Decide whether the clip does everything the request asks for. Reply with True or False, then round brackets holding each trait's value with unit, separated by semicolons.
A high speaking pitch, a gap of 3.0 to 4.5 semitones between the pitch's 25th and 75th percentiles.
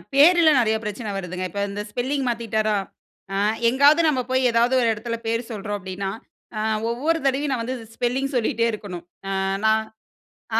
True (230 Hz; 3.7 semitones)